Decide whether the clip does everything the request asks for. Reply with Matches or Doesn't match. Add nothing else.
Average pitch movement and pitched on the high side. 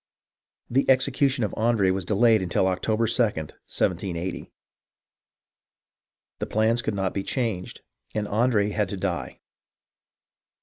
Doesn't match